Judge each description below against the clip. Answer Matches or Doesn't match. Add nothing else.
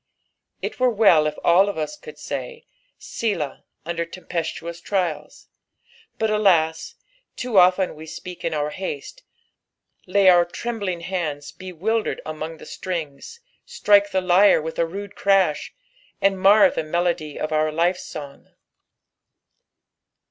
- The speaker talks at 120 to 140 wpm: Matches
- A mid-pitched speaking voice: Matches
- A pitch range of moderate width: Matches